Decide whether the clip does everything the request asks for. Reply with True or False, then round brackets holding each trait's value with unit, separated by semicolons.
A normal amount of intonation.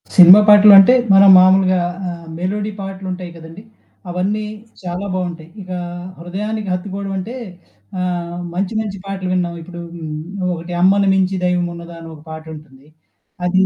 False (2.1 semitones)